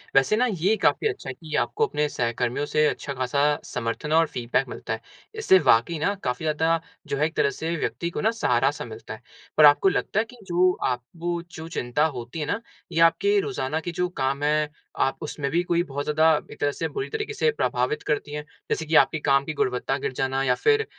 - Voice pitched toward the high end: No, medium, 150 Hz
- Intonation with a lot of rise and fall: No, average, 4.4 semitones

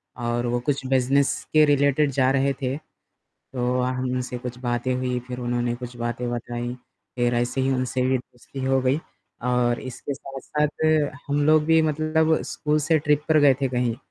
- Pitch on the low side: Yes, low, 130 Hz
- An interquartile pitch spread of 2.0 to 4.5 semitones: Yes, average, 2.8 semitones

